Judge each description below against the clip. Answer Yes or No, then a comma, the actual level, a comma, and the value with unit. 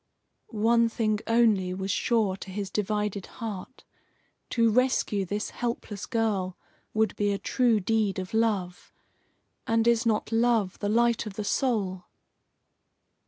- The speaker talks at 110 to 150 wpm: Yes, slow, 135 wpm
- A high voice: Yes, high, 215 Hz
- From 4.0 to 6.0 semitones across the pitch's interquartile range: No, narrow, 2.6 semitones